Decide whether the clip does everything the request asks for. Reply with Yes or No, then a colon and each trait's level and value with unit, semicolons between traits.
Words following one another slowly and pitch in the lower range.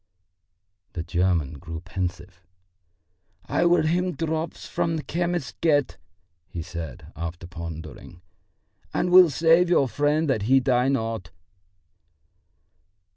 Yes: slow, 115 wpm; low, 125 Hz